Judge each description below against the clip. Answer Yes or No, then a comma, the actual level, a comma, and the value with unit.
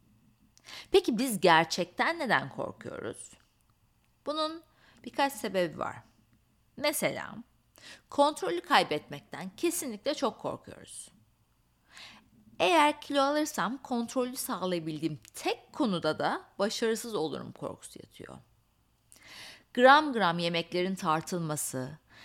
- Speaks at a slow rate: Yes, slow, 85 wpm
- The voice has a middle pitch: No, high, 225 Hz